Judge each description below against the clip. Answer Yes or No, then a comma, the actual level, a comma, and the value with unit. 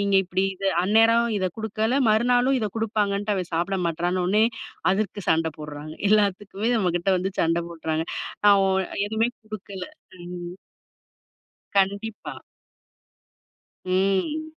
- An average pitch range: Yes, average, 3.4 semitones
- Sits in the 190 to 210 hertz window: Yes, high, 200 Hz